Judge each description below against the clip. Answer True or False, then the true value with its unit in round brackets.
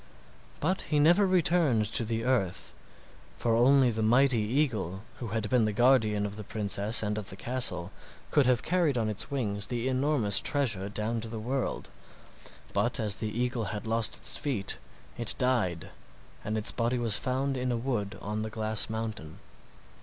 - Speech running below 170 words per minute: False (175 wpm)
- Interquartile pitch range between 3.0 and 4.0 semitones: True (3.4 semitones)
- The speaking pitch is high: False (115 Hz)